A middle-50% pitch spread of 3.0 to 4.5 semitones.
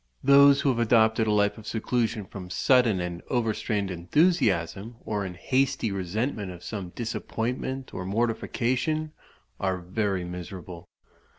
No: average, 5.0 semitones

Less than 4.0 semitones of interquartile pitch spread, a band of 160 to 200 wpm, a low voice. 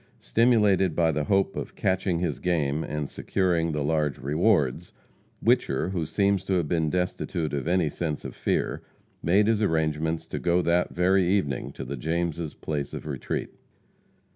Yes: average, 3.5 semitones; average, 165 wpm; very low, 85 Hz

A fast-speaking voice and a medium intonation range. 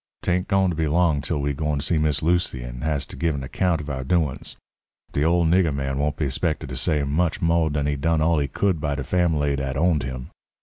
Yes: fast, 250 wpm; average, 3.1 semitones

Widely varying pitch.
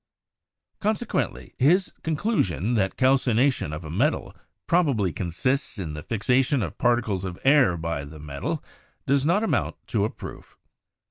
Yes: wide, 8.4 semitones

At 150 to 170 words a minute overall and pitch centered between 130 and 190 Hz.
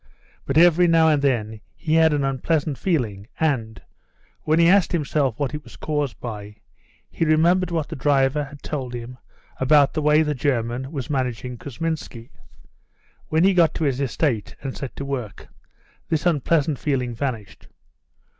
Yes: average, 165 wpm; medium, 140 Hz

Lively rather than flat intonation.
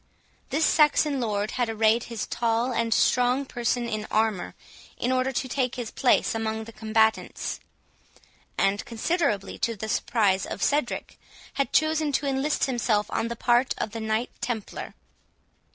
No: average, 2.9 semitones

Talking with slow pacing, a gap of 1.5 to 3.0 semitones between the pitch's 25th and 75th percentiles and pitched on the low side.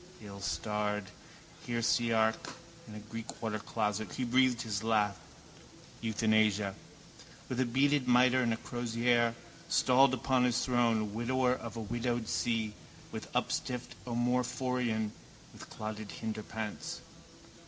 Yes: slow, 110 wpm; narrow, 2.4 semitones; low, 115 Hz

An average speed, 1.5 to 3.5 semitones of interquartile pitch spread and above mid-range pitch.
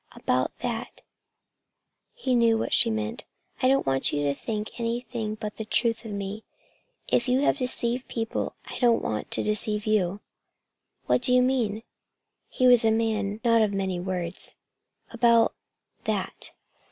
Yes: average, 160 wpm; narrow, 2.5 semitones; high, 225 Hz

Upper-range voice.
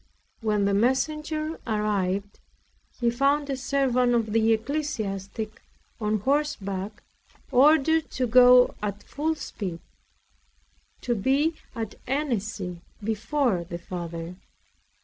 Yes: high, 230 Hz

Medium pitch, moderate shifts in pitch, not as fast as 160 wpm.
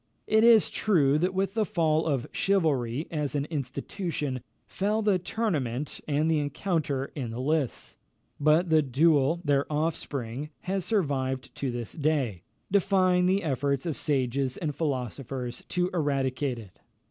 Yes: medium, 150 Hz; average, 5.0 semitones; average, 145 wpm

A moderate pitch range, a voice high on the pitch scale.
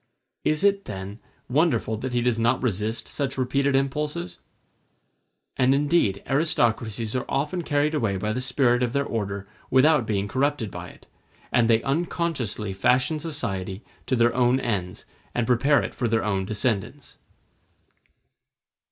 No: average, 4.6 semitones; low, 125 Hz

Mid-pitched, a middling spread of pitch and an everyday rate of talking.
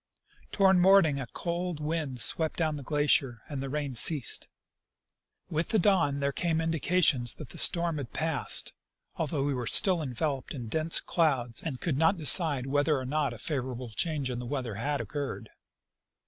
Yes: medium, 145 Hz; average, 3.8 semitones; average, 175 wpm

